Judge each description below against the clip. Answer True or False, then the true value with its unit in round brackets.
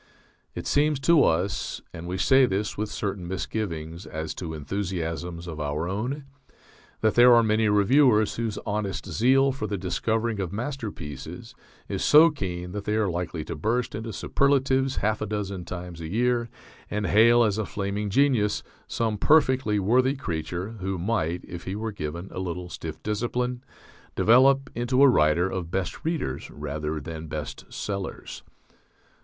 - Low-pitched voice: True (105 Hz)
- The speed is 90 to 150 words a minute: False (160 wpm)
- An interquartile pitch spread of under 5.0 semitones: False (5.5 semitones)